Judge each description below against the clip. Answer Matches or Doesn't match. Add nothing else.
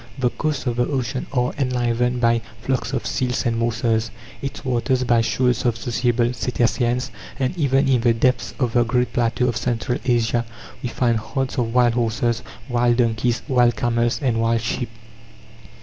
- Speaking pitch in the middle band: Doesn't match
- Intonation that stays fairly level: Matches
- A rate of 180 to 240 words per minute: Doesn't match